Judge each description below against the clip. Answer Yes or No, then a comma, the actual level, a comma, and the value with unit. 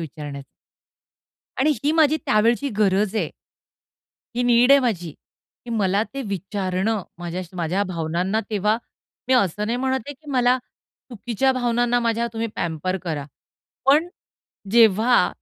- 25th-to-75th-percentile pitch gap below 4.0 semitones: No, average, 4.9 semitones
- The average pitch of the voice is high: Yes, high, 220 Hz